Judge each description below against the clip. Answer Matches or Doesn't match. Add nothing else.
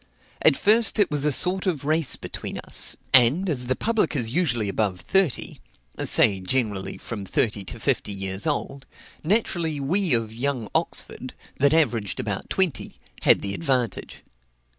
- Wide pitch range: Matches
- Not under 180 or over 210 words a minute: Doesn't match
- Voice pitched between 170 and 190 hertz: Doesn't match